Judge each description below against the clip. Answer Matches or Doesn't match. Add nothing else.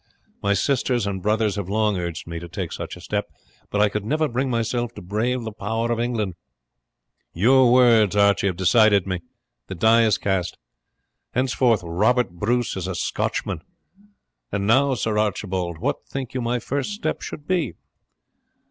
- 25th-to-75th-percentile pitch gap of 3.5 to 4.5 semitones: Matches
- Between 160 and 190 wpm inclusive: Matches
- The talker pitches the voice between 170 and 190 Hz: Doesn't match